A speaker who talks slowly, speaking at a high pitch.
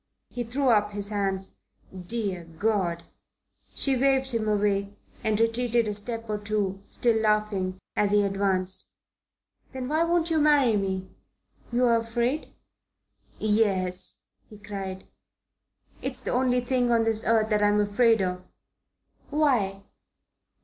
Yes: slow, 130 wpm; high, 215 Hz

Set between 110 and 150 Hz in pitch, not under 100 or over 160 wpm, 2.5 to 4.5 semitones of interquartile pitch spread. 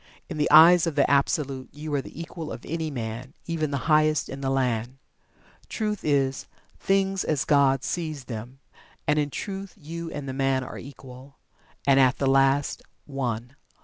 No: medium, 140 Hz; average, 175 wpm; average, 2.8 semitones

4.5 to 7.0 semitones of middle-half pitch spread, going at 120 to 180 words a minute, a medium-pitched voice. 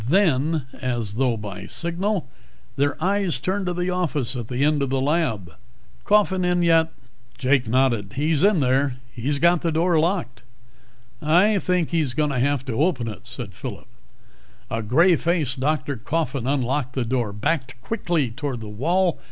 Yes: average, 5.2 semitones; average, 170 wpm; medium, 145 Hz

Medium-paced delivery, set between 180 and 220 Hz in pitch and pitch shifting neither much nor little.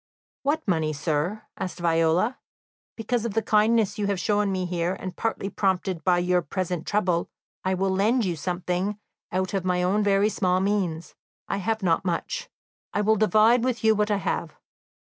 Yes: average, 180 wpm; high, 190 Hz; average, 3.1 semitones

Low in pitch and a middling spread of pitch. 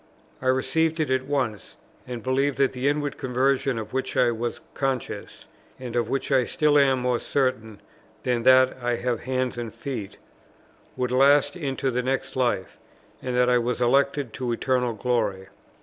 No: low, 130 Hz; narrow, 2.0 semitones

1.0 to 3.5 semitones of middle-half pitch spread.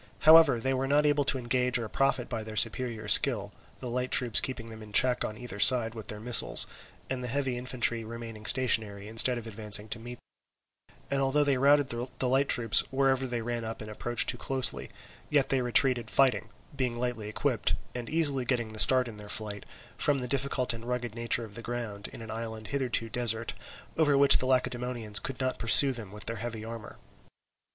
Yes: average, 2.7 semitones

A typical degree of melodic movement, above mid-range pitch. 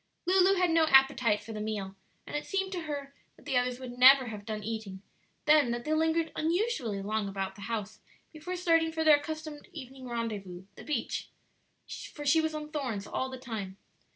No: wide, 6.3 semitones; very high, 265 Hz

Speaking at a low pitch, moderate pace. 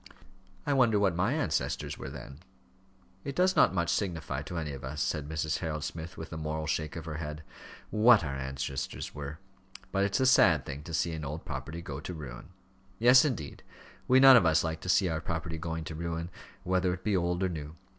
No: very low, 80 Hz; fast, 215 wpm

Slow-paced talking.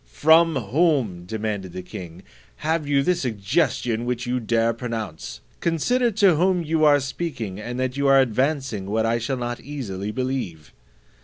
No: average, 160 wpm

